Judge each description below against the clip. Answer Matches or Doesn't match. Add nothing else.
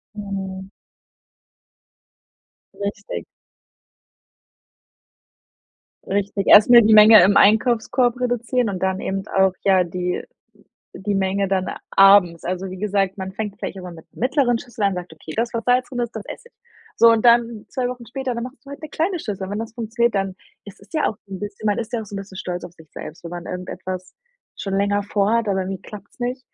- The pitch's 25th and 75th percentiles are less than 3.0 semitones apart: Doesn't match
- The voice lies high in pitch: Matches